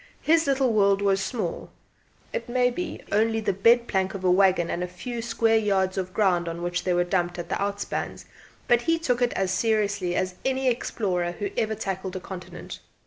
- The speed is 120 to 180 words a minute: No, average, 200 wpm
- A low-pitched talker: No, high, 200 Hz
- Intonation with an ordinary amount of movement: Yes, average, 4.2 semitones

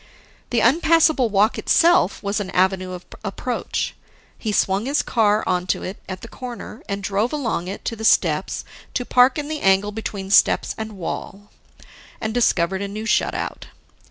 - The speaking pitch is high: Yes, high, 215 Hz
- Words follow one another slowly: No, average, 170 wpm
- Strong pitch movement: No, average, 3.9 semitones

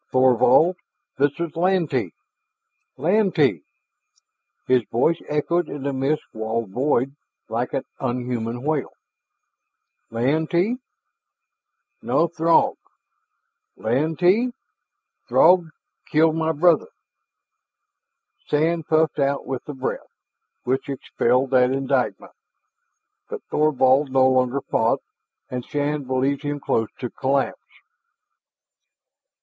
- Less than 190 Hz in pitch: Yes, medium, 140 Hz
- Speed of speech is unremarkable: No, slow, 100 wpm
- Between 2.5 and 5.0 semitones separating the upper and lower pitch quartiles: Yes, average, 3.8 semitones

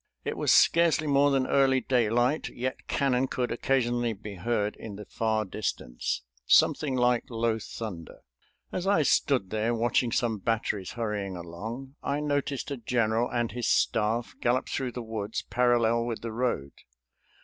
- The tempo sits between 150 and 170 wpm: Yes, average, 155 wpm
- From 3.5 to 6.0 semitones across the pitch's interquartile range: No, average, 3.0 semitones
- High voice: No, low, 120 Hz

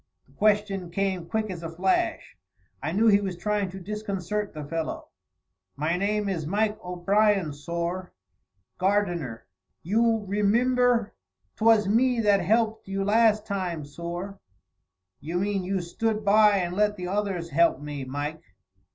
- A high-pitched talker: Yes, high, 195 Hz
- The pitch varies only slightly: No, average, 3.5 semitones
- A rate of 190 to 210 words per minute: No, average, 145 wpm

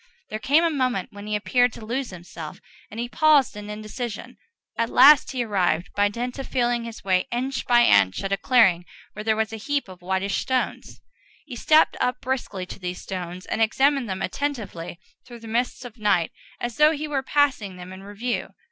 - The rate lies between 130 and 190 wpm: No, fast, 205 wpm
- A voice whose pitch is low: No, high, 225 Hz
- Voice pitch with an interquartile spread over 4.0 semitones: Yes, average, 4.8 semitones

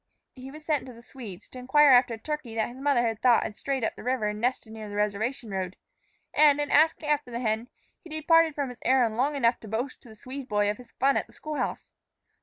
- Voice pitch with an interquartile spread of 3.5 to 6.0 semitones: Yes, average, 4.3 semitones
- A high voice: Yes, very high, 250 Hz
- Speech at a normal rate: No, fast, 250 wpm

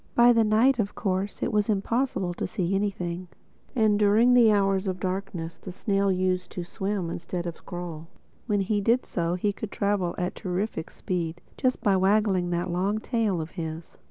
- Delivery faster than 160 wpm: Yes, average, 185 wpm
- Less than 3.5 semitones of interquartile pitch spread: Yes, average, 3.0 semitones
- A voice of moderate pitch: No, high, 195 Hz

